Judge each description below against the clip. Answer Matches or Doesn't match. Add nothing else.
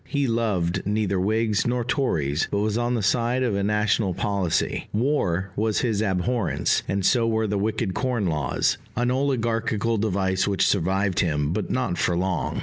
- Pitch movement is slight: Doesn't match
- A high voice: Doesn't match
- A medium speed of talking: Matches